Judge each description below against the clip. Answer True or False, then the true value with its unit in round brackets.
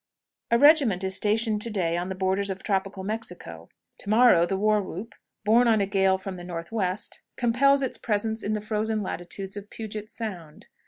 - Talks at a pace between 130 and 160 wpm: False (190 wpm)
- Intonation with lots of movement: False (2.8 semitones)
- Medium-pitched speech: False (205 Hz)